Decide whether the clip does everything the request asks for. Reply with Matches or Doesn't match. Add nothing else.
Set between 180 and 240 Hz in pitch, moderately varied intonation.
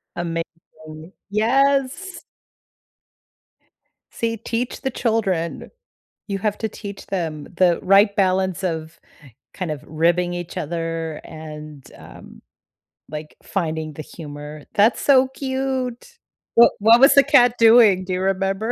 Doesn't match